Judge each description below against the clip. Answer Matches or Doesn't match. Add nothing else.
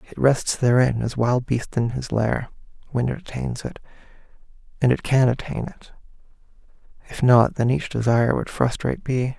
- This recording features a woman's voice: Doesn't match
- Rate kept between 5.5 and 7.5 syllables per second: Doesn't match